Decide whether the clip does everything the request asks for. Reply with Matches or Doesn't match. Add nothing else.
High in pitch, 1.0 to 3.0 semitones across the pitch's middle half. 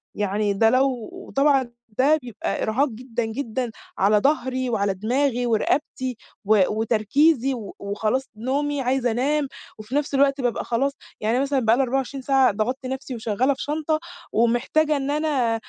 Doesn't match